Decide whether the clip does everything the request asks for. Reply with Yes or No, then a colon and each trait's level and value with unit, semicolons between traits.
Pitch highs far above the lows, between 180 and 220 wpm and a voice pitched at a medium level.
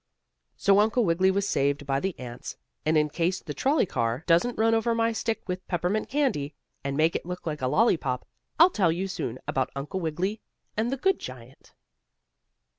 Yes: wide, 7.4 semitones; average, 190 wpm; medium, 180 Hz